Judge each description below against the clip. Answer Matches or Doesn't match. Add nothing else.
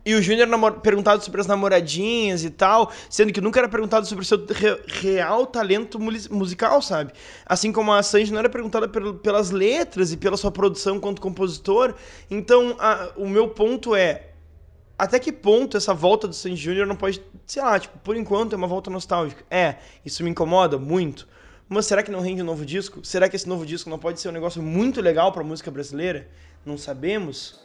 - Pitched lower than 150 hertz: Doesn't match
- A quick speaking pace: Matches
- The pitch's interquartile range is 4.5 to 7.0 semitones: Doesn't match